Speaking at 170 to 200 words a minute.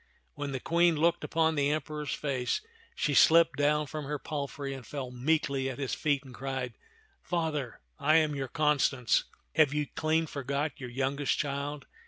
Yes: average, 180 wpm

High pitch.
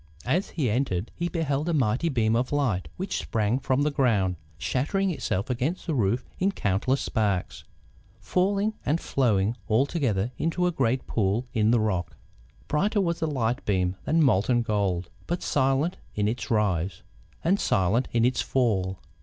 No: low, 120 Hz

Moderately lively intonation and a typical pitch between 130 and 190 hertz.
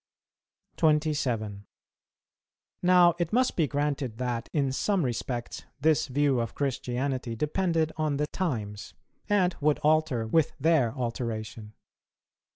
Yes: average, 4.9 semitones; medium, 140 Hz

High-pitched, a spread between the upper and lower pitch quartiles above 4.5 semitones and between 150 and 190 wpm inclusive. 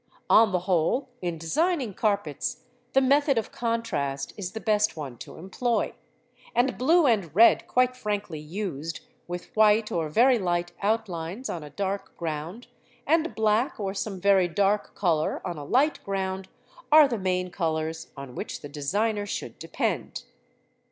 Yes: high, 200 Hz; average, 5.3 semitones; average, 155 wpm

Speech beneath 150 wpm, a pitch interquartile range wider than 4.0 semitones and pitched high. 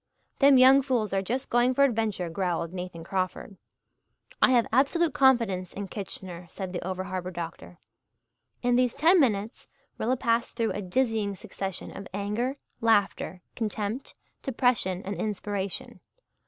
Yes: average, 140 wpm; average, 4.8 semitones; high, 210 Hz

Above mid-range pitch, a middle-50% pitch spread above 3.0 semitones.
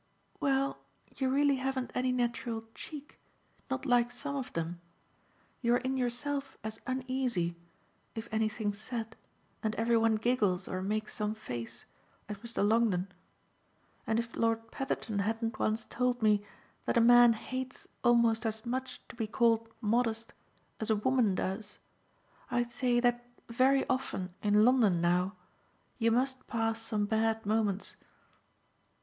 No: high, 230 Hz; average, 2.7 semitones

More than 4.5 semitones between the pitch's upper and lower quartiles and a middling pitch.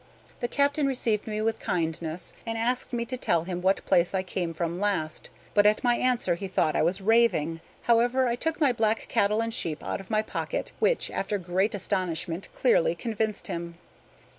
No: average, 5.2 semitones; high, 210 Hz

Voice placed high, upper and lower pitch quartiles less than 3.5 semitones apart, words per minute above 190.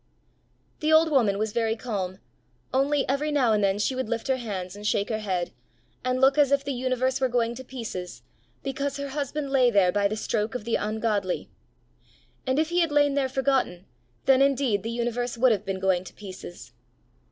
No: high, 245 Hz; average, 4.7 semitones; average, 200 wpm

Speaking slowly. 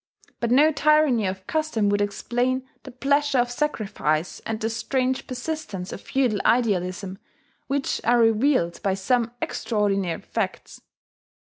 Yes: slow, 130 wpm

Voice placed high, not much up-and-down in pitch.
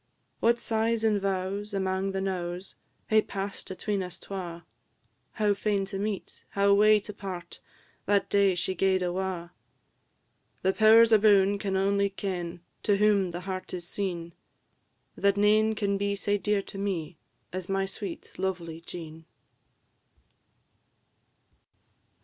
Yes: high, 195 Hz; narrow, 1.7 semitones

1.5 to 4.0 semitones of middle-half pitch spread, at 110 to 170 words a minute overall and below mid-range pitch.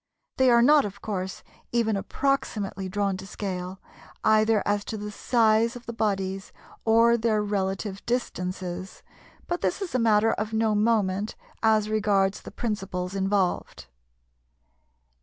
No: average, 2.8 semitones; average, 140 wpm; high, 210 Hz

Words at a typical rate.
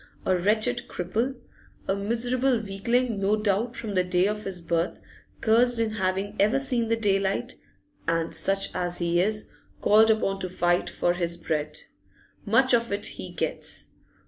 Yes: average, 160 wpm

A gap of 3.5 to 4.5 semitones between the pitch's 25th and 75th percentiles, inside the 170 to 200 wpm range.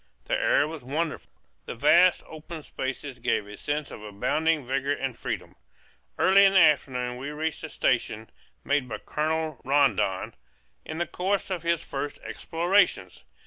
No: average, 4.2 semitones; average, 155 wpm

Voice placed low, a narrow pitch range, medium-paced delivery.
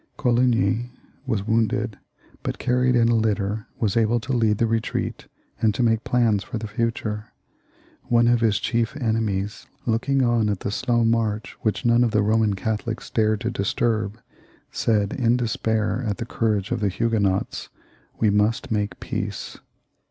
Yes: low, 110 Hz; narrow, 1.9 semitones; average, 165 wpm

